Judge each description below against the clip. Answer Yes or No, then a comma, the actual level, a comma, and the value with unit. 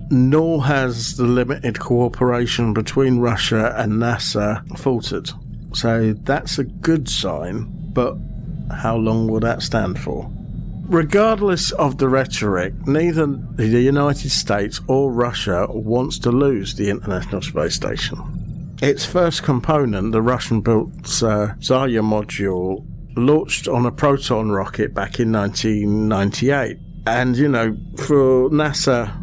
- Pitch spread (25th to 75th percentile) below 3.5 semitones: No, average, 4.5 semitones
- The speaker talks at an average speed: No, slow, 120 wpm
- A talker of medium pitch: No, low, 125 Hz